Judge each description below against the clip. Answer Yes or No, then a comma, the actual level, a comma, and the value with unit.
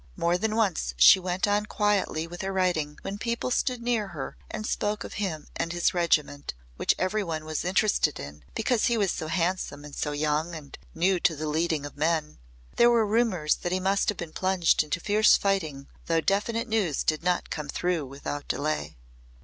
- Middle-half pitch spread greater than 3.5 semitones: Yes, average, 4.9 semitones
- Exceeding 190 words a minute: Yes, average, 200 wpm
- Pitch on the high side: No, medium, 175 Hz